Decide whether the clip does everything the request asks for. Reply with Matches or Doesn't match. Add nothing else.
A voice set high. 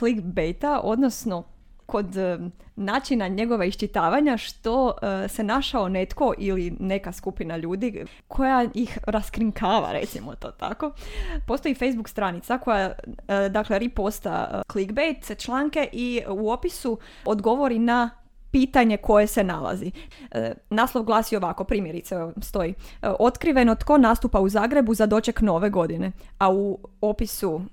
Matches